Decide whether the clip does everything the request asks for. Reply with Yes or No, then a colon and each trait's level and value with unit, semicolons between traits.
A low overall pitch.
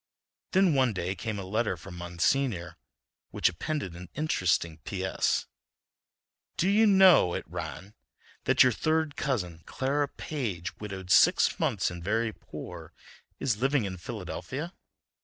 Yes: low, 105 Hz